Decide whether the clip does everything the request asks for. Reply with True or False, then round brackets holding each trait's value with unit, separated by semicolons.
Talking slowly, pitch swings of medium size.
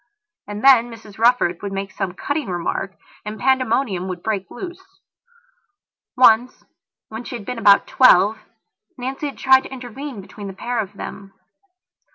False (155 wpm; 4.8 semitones)